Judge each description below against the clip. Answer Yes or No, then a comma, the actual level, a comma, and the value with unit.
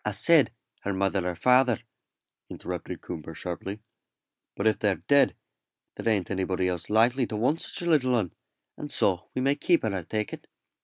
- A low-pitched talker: Yes, low, 105 Hz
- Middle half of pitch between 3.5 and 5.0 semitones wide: No, wide, 5.5 semitones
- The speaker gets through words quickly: No, average, 185 wpm